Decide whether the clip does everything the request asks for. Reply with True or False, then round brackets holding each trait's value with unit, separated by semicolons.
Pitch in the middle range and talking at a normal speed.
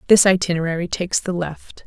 True (180 Hz; 160 wpm)